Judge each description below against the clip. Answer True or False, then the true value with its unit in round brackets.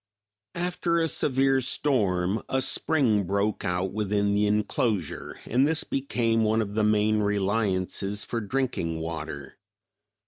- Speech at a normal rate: False (130 wpm)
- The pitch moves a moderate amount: True (4.7 semitones)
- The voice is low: True (105 Hz)